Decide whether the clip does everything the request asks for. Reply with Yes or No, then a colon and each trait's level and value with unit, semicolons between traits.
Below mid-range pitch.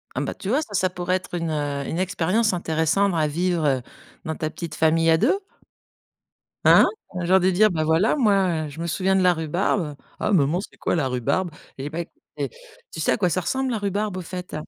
No: medium, 175 Hz